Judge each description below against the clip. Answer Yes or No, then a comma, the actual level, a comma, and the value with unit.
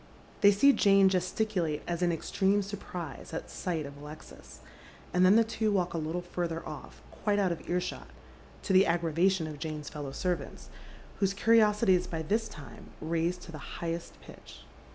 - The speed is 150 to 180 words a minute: Yes, average, 175 wpm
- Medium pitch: Yes, medium, 180 Hz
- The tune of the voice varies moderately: Yes, average, 3.5 semitones